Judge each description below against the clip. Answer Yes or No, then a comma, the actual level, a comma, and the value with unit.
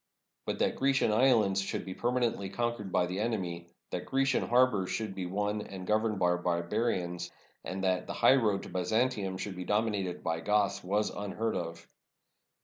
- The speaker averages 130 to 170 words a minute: Yes, average, 165 wpm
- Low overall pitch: Yes, low, 100 Hz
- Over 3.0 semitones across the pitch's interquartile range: Yes, average, 3.6 semitones